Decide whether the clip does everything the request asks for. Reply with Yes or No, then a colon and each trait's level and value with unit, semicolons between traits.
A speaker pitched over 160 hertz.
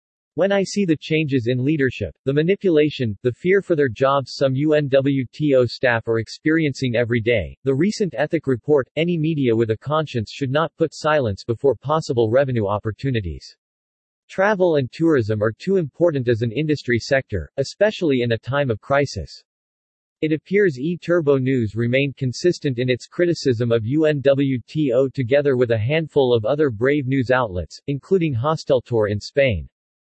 No: low, 135 Hz